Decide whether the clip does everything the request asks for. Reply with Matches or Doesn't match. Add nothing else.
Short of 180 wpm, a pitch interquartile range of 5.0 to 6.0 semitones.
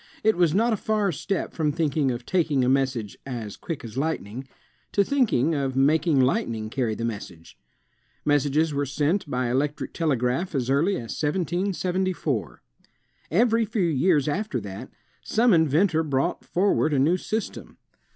Matches